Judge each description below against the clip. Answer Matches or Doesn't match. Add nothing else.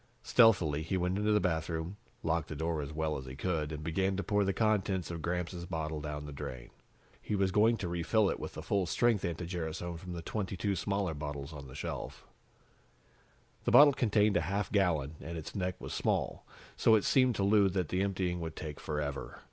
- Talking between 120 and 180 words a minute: Doesn't match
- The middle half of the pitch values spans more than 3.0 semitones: Matches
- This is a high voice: Doesn't match